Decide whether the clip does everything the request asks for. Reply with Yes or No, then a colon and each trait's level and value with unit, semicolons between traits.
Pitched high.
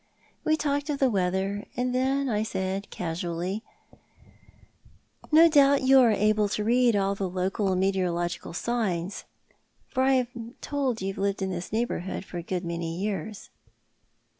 Yes: high, 205 Hz